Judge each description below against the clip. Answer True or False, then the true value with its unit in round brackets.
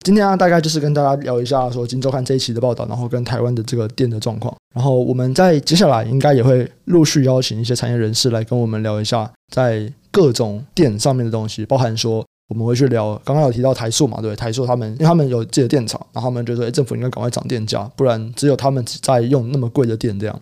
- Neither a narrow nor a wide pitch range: True (3.1 semitones)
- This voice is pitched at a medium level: False (125 Hz)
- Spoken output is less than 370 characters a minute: False (400 characters per minute)